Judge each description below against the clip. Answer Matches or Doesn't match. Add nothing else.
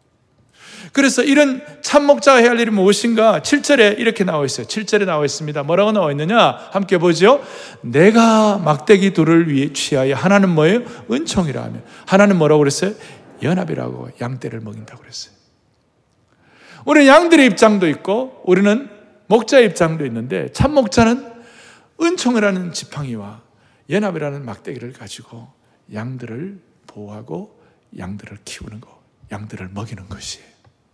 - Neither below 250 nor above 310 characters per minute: Doesn't match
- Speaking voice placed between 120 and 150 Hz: Doesn't match